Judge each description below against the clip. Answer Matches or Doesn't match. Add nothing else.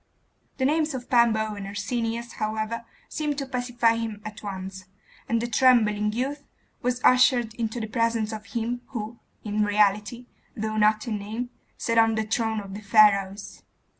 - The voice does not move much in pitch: Matches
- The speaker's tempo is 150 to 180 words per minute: Matches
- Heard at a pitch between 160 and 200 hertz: Doesn't match